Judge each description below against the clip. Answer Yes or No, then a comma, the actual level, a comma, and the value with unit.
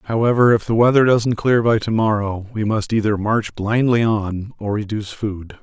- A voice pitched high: No, low, 110 Hz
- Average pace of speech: Yes, average, 190 wpm